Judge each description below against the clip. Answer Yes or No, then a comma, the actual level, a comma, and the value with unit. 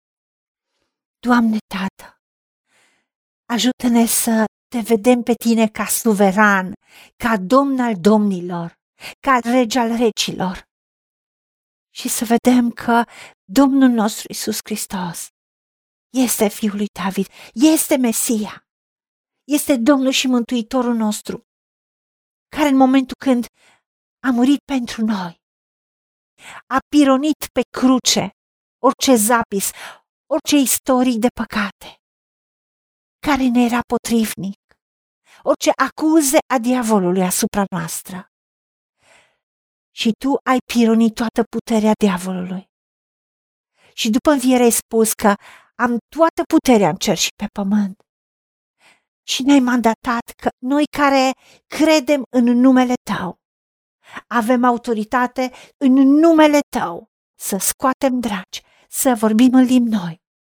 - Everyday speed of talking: No, slow, 110 wpm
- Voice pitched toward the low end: No, high, 240 Hz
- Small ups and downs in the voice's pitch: No, average, 3.5 semitones